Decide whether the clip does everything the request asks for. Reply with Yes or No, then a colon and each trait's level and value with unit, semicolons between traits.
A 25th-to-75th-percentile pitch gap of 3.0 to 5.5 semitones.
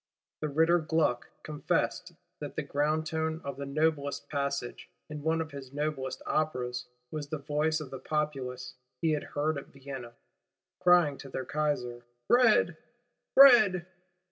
No: narrow, 2.6 semitones